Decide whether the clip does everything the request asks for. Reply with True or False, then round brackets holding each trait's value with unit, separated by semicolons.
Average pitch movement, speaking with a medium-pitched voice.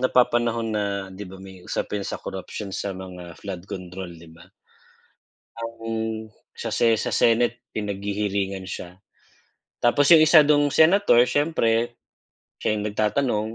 False (3.5 semitones; 110 Hz)